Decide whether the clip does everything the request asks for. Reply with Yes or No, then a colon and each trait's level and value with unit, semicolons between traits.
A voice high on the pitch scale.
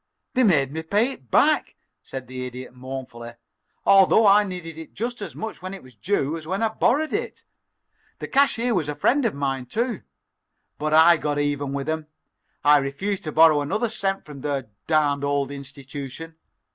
No: medium, 155 Hz